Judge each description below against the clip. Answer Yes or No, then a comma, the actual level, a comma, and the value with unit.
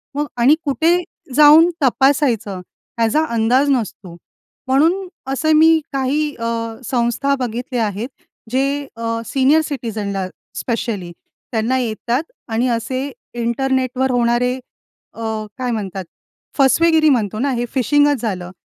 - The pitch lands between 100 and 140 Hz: No, very high, 250 Hz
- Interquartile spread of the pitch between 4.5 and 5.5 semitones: No, average, 3.7 semitones